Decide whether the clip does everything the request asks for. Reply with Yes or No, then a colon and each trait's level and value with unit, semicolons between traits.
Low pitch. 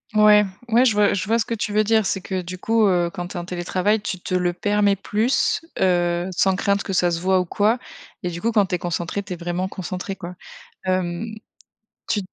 No: high, 190 Hz